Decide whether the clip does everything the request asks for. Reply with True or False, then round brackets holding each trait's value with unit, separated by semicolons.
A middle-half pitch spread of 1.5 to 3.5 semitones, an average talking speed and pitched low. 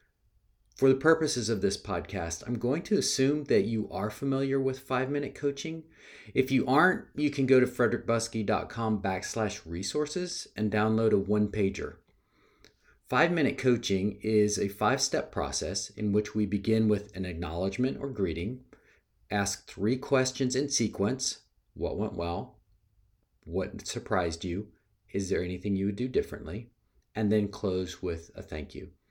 False (4.6 semitones; 150 wpm; 110 Hz)